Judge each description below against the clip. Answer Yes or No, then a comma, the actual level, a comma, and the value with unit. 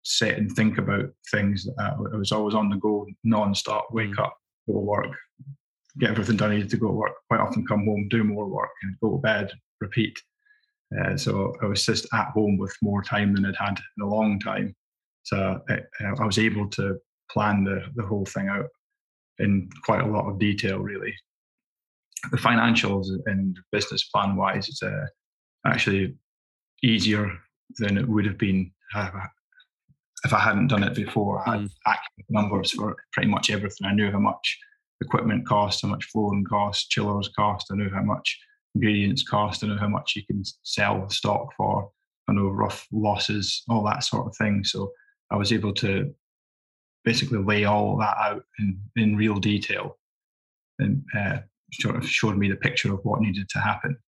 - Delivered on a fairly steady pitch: Yes, narrow, 2.0 semitones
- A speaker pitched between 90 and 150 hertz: Yes, low, 105 Hz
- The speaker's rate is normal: Yes, average, 185 wpm